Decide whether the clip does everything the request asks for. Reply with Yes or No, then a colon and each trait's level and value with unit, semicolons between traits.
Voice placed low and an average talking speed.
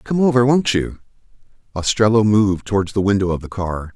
Yes: low, 105 Hz; average, 180 wpm